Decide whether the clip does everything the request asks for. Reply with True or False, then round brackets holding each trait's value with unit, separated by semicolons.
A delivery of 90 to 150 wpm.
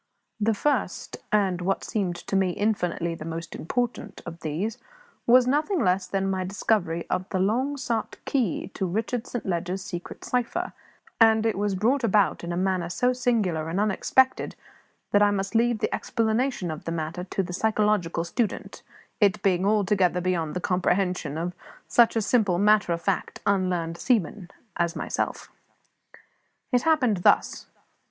False (160 wpm)